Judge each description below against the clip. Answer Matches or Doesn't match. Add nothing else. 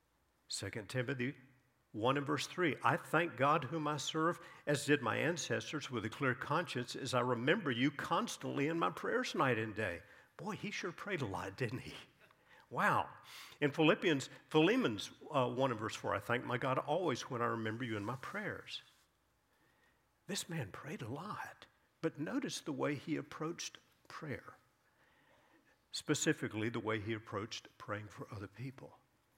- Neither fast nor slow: Matches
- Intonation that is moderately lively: Matches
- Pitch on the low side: Matches